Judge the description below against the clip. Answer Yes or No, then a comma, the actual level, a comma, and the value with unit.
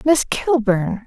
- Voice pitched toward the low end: No, high, 245 Hz